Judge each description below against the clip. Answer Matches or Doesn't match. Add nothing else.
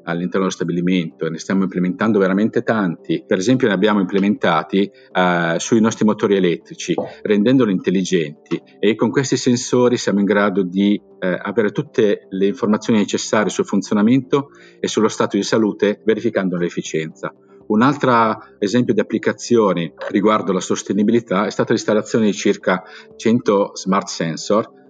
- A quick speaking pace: Doesn't match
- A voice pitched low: Matches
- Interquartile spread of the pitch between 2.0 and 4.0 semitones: Matches